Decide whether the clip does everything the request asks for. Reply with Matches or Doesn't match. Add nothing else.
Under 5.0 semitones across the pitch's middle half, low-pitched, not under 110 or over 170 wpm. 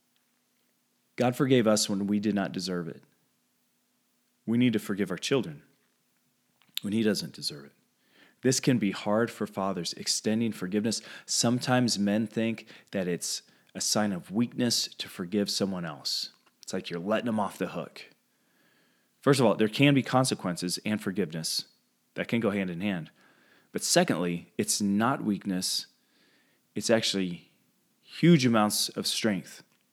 Matches